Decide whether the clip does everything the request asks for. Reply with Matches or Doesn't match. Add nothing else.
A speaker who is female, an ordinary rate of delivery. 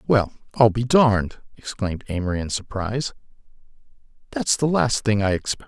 Doesn't match